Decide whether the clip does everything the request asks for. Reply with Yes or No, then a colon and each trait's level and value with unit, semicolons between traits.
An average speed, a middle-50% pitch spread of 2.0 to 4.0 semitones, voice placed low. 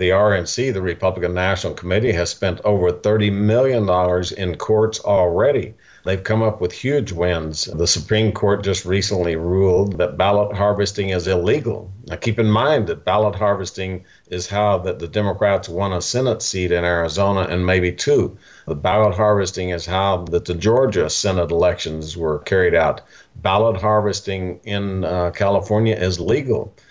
Yes: average, 160 wpm; average, 2.9 semitones; very low, 95 Hz